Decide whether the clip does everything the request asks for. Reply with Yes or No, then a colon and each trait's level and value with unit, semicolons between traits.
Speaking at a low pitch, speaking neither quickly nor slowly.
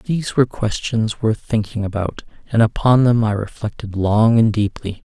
Yes: low, 110 Hz; average, 165 wpm